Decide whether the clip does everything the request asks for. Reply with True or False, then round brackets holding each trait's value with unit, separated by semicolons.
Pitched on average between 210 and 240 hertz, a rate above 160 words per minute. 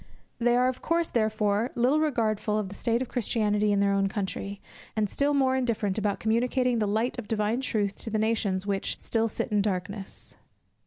True (220 Hz; 195 wpm)